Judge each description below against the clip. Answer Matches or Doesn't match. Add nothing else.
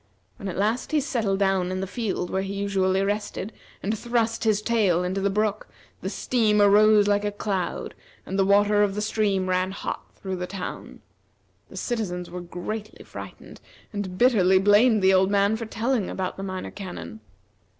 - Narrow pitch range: Matches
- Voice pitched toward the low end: Doesn't match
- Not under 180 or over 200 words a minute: Matches